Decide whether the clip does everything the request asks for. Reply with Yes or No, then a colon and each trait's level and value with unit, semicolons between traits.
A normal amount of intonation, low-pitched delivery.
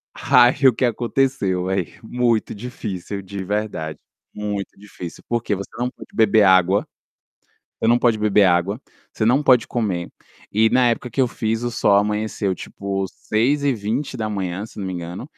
Yes: average, 3.6 semitones; low, 105 Hz